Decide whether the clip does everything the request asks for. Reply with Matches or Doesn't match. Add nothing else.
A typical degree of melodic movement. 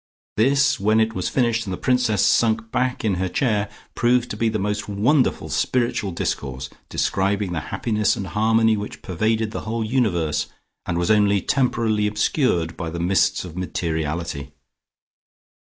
Matches